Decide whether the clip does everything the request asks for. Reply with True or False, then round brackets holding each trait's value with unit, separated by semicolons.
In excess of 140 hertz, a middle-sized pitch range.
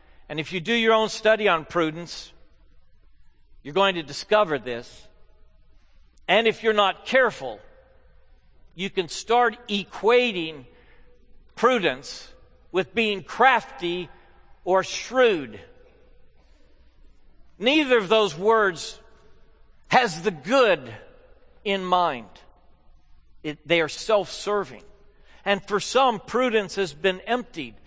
False (190 Hz; 8.7 semitones)